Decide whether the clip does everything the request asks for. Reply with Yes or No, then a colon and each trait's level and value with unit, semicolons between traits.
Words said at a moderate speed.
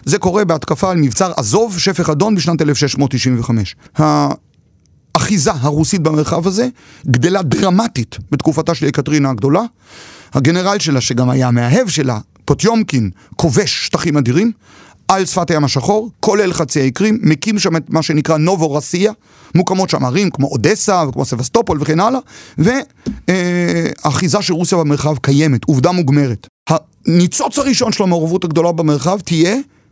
Yes: average, 135 wpm